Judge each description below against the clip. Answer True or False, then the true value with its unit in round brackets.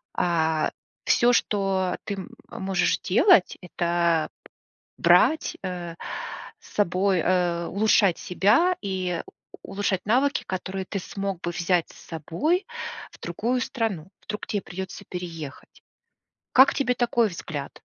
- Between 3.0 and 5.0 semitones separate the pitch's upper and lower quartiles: True (3.5 semitones)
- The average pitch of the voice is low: False (190 Hz)